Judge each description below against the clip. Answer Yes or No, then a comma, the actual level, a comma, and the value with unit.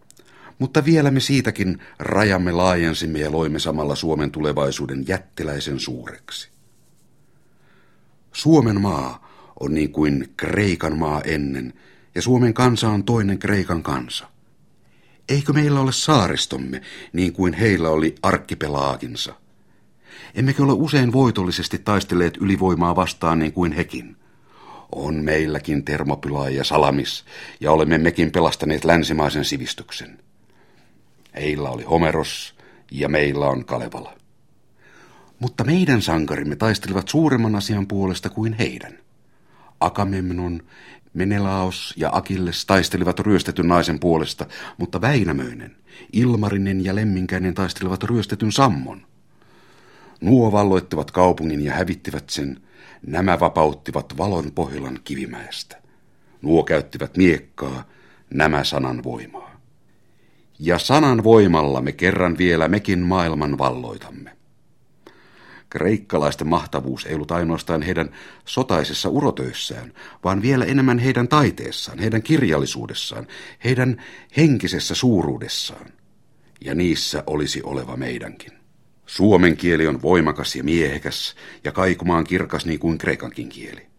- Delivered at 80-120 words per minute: Yes, average, 110 wpm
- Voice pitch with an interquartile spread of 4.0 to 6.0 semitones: Yes, average, 5.2 semitones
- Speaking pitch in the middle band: No, very low, 90 Hz